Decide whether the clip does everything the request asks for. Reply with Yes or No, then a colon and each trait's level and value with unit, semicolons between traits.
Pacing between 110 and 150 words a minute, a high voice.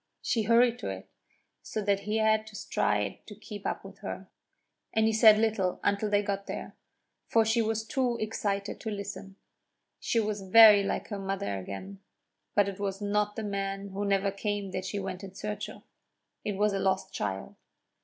No: average, 190 wpm; high, 205 Hz